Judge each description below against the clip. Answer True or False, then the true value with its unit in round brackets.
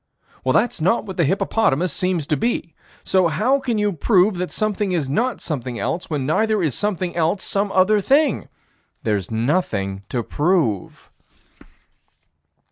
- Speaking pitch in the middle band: True (180 Hz)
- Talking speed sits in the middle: True (145 wpm)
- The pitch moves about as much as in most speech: False (6.1 semitones)